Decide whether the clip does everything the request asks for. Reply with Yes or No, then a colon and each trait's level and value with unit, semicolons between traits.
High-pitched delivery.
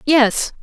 Yes: very high, 260 Hz